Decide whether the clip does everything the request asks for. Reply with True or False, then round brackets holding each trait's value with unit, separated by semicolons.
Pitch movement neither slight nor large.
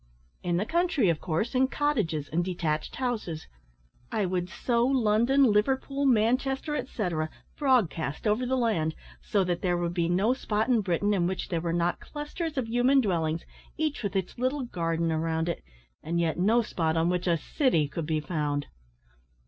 False (7.1 semitones)